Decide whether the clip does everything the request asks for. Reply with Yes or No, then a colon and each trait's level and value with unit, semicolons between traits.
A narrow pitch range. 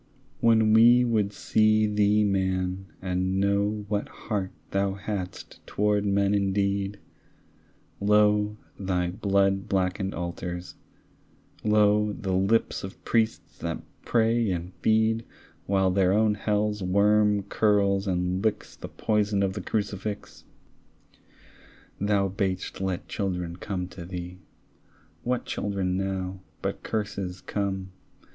Yes: narrow, 1.9 semitones